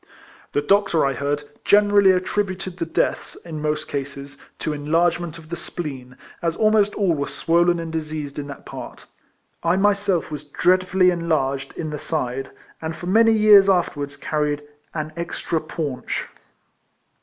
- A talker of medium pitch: Yes, medium, 165 Hz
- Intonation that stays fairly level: No, average, 4.0 semitones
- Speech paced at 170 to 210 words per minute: No, average, 155 wpm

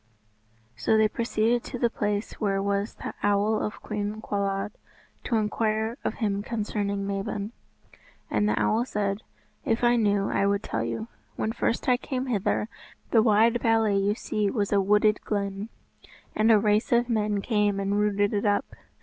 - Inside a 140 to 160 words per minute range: No, average, 170 wpm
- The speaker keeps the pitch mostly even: Yes, narrow, 1.7 semitones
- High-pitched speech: Yes, high, 210 Hz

